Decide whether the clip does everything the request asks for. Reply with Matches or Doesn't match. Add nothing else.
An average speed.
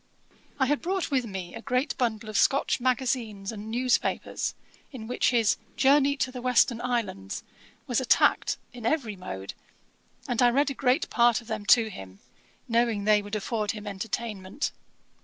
Matches